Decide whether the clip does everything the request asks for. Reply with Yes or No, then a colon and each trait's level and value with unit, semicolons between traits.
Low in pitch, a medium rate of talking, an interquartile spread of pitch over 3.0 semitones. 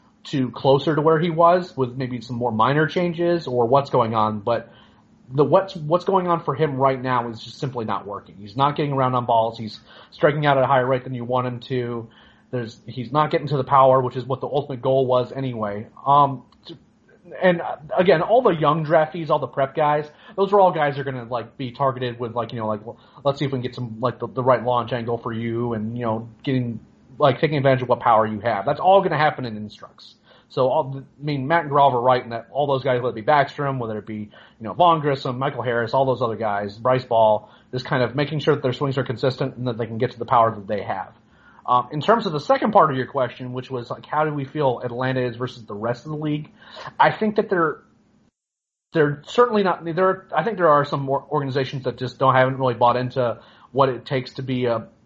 No: low, 130 Hz; fast, 255 wpm; average, 3.6 semitones